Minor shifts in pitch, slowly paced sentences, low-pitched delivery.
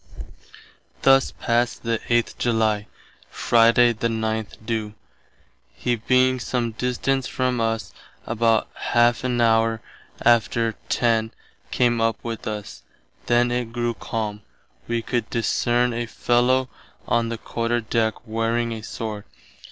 Yes: narrow, 1.2 semitones; slow, 125 wpm; low, 115 Hz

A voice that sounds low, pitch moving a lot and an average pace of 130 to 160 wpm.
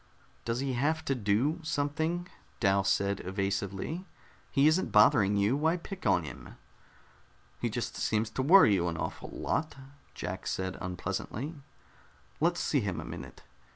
Yes: low, 120 Hz; wide, 7.9 semitones; average, 150 wpm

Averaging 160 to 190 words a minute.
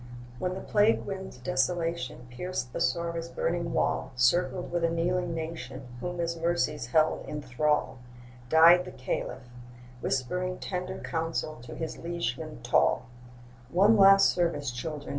No: slow, 135 wpm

